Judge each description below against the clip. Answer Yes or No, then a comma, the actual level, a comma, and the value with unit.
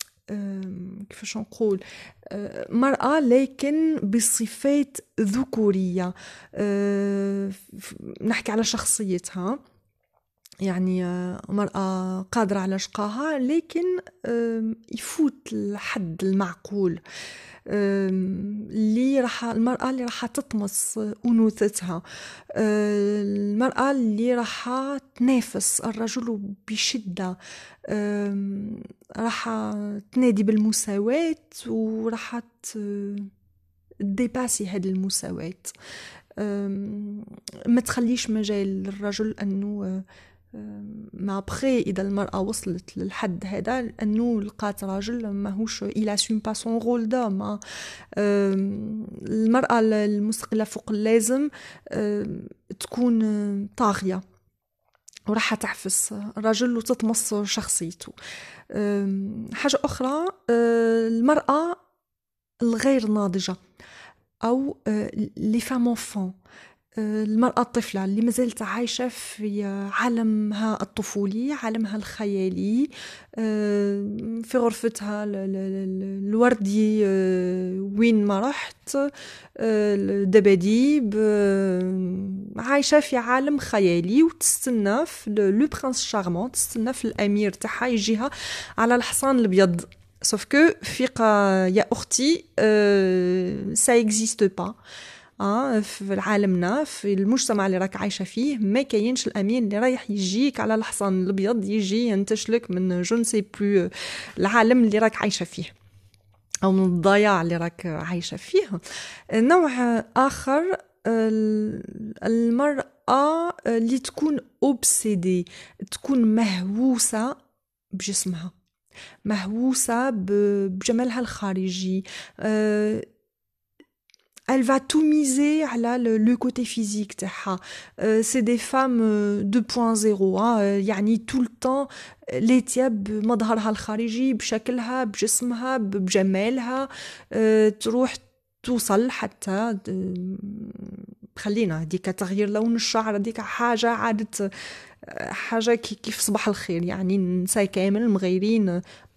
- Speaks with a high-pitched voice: Yes, high, 215 Hz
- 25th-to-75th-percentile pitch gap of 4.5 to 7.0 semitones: No, average, 3.2 semitones